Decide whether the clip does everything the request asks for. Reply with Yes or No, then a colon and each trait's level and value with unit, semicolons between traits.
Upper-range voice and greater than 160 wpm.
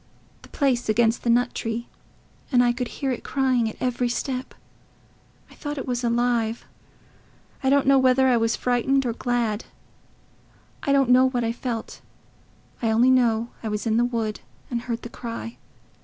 Yes: high, 240 Hz; average, 175 wpm